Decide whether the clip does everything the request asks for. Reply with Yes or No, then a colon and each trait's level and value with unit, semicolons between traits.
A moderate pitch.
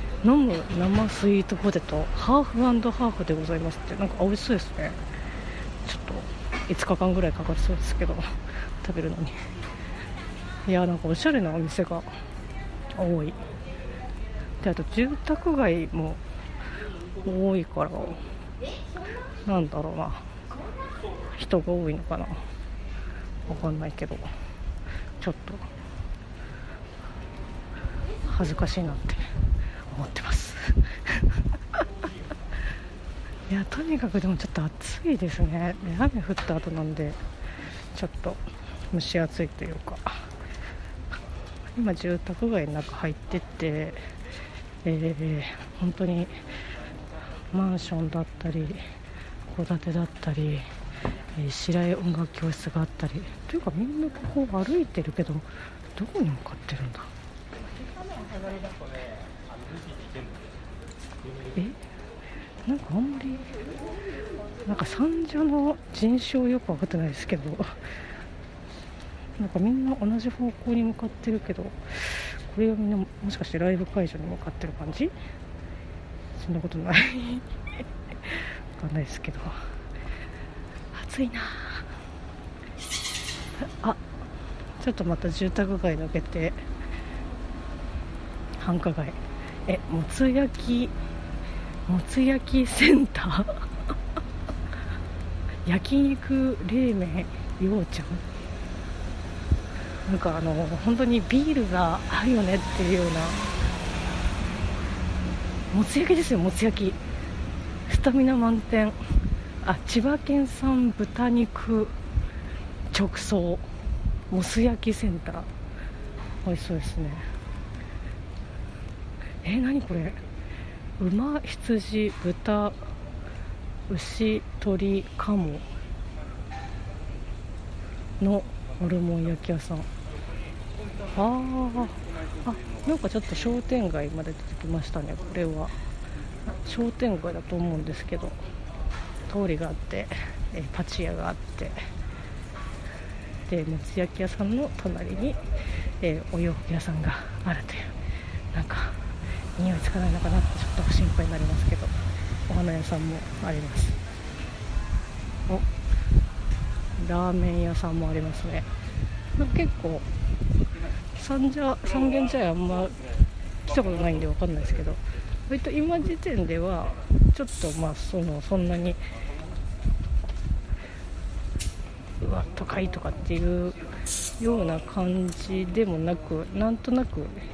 Yes: medium, 155 Hz